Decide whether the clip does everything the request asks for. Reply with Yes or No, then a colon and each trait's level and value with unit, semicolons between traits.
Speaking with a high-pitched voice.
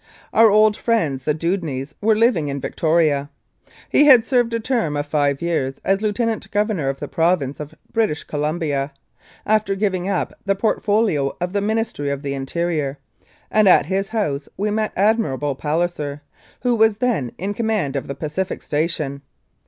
No: medium, 175 Hz